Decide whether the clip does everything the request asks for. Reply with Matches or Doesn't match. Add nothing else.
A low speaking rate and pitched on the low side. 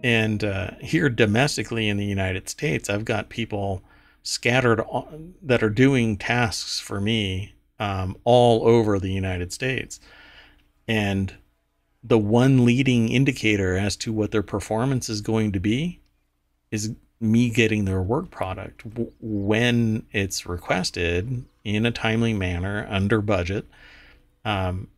Matches